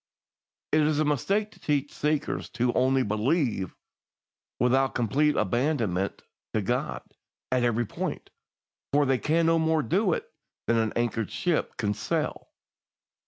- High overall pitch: No, low, 135 Hz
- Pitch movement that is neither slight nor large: Yes, average, 4.7 semitones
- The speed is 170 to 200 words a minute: No, average, 140 wpm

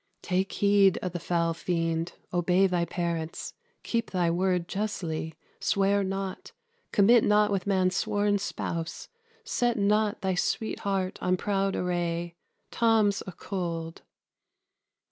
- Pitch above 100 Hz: Yes, high, 190 Hz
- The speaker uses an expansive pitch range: No, average, 2.8 semitones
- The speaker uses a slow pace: Yes, slow, 130 wpm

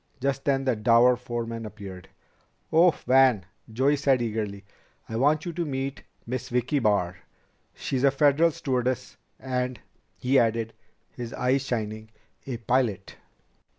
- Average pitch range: Yes, average, 3.2 semitones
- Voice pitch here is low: Yes, low, 125 Hz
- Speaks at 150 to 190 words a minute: No, average, 140 wpm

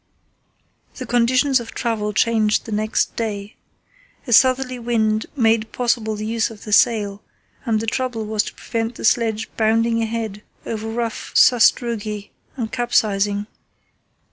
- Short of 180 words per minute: Yes, average, 140 wpm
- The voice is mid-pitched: No, high, 225 Hz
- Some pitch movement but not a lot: No, narrow, 1.6 semitones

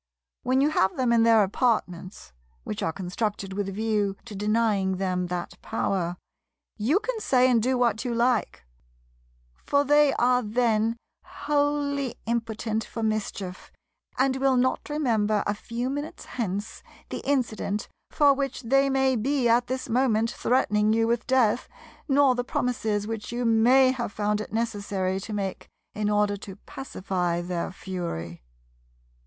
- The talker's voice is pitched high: Yes, high, 225 Hz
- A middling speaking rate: Yes, average, 150 wpm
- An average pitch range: Yes, average, 4.2 semitones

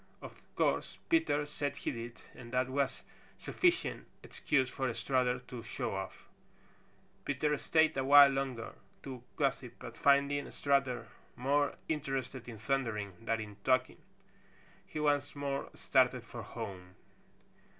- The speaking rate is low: Yes, slow, 130 wpm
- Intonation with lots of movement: No, average, 2.9 semitones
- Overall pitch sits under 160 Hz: Yes, low, 135 Hz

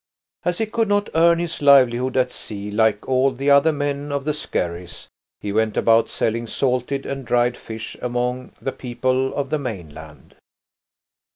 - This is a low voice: Yes, low, 130 Hz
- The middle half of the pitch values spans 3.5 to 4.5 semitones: Yes, average, 3.9 semitones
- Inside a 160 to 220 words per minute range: Yes, average, 165 wpm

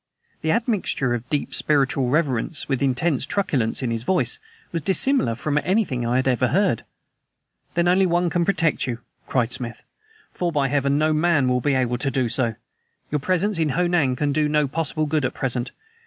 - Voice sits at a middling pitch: Yes, medium, 145 Hz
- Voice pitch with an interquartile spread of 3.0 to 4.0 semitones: No, average, 5.2 semitones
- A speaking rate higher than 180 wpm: Yes, average, 190 wpm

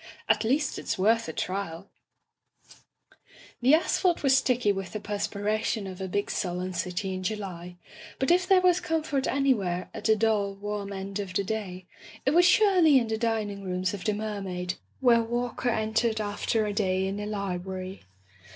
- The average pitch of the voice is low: No, high, 210 Hz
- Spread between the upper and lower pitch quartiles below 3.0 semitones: No, average, 3.9 semitones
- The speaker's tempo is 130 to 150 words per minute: No, average, 175 wpm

